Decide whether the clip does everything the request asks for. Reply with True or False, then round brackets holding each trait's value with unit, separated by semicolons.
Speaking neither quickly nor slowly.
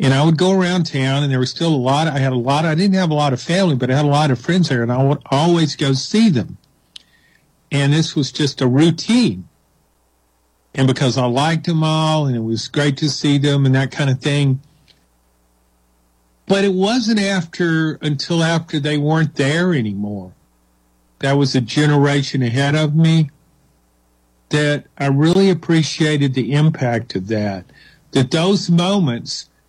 True (180 wpm)